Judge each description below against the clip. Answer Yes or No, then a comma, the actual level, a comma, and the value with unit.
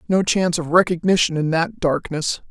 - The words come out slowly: No, average, 170 wpm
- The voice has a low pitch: No, medium, 170 Hz